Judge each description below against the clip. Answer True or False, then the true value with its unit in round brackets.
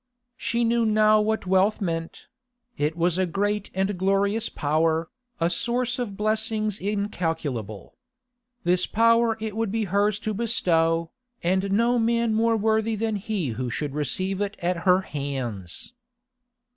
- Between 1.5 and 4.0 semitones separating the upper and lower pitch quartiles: False (4.7 semitones)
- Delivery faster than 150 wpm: False (145 wpm)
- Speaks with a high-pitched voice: True (200 Hz)